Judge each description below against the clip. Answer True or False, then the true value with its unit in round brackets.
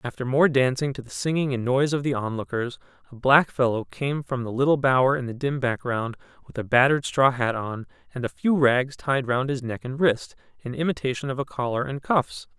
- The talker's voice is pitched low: True (130 Hz)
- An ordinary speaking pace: False (220 wpm)